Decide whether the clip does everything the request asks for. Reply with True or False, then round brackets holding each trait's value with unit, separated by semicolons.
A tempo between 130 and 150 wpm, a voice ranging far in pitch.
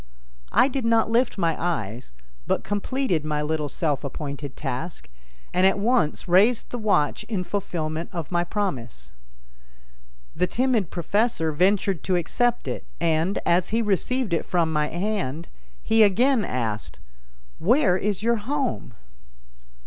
True (140 wpm; 6.0 semitones)